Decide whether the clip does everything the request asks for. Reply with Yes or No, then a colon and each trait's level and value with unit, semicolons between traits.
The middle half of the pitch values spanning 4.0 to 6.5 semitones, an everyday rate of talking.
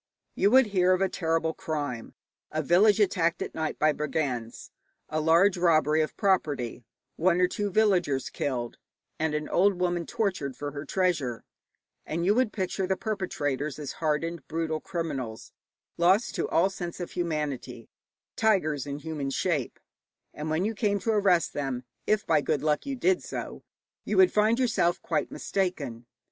Yes: average, 4.6 semitones; average, 165 wpm